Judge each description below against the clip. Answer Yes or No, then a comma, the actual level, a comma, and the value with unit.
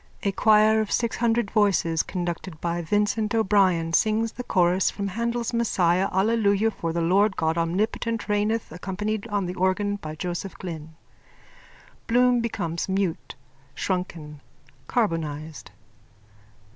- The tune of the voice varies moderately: Yes, average, 4.2 semitones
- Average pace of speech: No, slow, 125 wpm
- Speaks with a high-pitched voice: Yes, high, 195 Hz